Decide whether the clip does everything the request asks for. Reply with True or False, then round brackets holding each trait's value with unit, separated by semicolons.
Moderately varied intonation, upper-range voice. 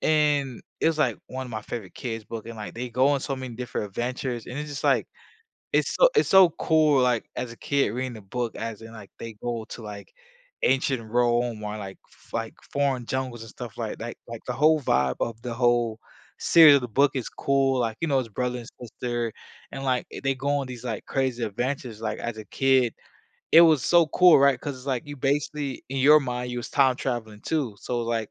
False (3.0 semitones; 125 Hz)